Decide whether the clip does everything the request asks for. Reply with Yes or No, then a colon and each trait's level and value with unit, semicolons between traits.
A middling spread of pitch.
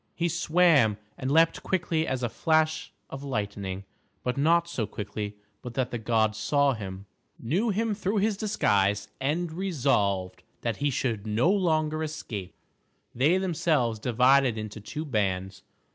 No: wide, 7.5 semitones